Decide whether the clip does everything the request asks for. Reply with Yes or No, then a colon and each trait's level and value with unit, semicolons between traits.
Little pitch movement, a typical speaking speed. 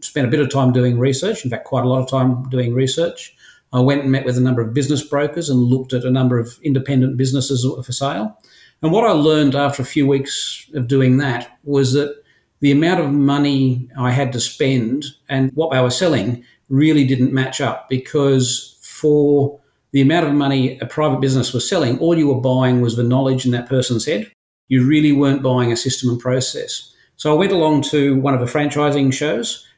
No: narrow, 2.1 semitones; fast, 215 wpm